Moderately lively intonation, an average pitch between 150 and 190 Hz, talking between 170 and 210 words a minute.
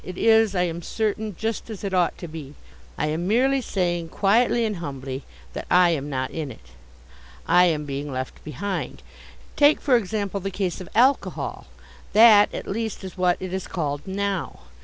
Yes: average, 4.8 semitones; medium, 185 Hz; average, 180 wpm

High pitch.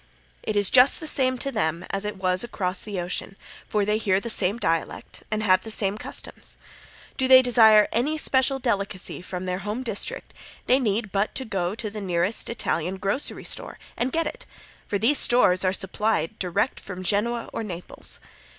Yes: high, 210 Hz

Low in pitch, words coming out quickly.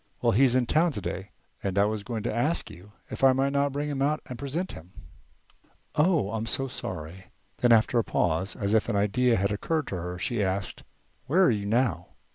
Yes: low, 115 Hz; fast, 215 wpm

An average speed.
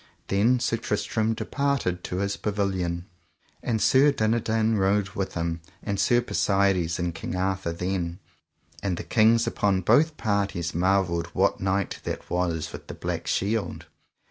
Yes: average, 145 wpm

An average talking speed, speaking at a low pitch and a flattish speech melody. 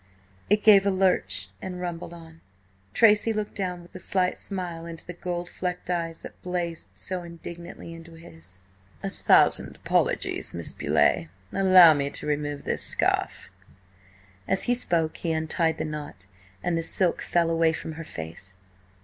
No: average, 160 wpm; medium, 170 Hz; narrow, 2.1 semitones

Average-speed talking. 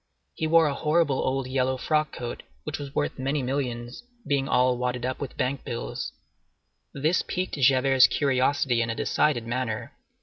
Yes: average, 160 wpm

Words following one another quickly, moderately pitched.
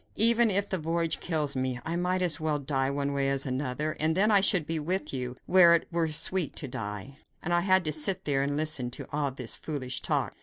Yes: fast, 235 wpm; medium, 155 Hz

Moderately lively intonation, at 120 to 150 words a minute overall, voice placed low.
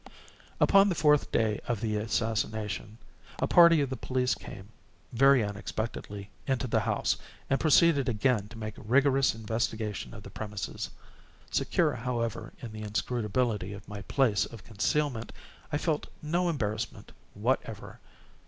Yes: average, 4.3 semitones; average, 140 wpm; low, 115 Hz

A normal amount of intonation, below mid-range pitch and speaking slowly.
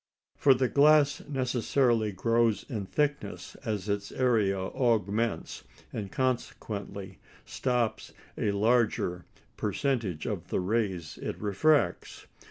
Yes: average, 4.3 semitones; low, 115 Hz; slow, 105 wpm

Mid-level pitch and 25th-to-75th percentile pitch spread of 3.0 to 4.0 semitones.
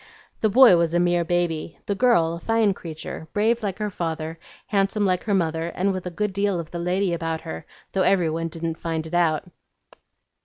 Yes: medium, 175 Hz; average, 3.3 semitones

